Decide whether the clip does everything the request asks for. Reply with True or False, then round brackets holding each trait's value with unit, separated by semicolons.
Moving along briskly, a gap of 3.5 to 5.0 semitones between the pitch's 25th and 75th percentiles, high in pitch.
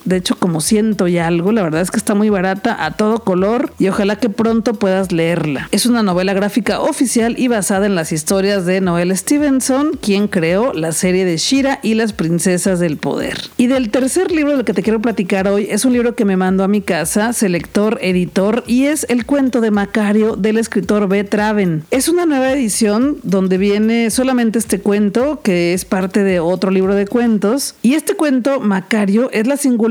True (205 wpm; 4.1 semitones; 215 Hz)